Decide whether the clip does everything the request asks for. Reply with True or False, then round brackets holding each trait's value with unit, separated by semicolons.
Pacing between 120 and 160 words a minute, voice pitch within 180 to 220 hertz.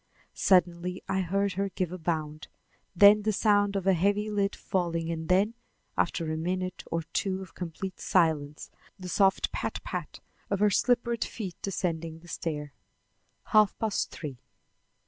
True (155 wpm; 185 Hz)